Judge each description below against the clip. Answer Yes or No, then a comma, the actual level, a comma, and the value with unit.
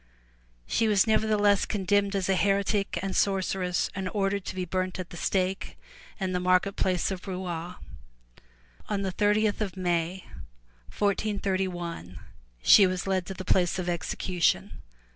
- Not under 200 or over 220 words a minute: No, average, 155 wpm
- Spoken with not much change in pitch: Yes, narrow, 1.8 semitones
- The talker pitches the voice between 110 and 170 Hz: No, high, 190 Hz